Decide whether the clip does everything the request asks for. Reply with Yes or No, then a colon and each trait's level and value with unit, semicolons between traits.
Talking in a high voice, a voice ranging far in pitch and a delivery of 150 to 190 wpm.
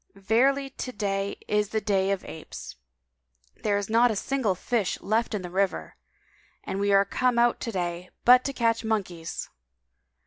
No: high, 210 Hz; average, 3.5 semitones; average, 170 wpm